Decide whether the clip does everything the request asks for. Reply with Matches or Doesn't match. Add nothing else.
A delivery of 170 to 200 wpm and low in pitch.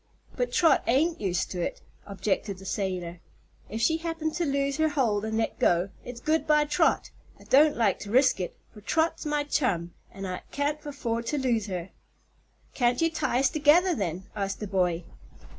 Doesn't match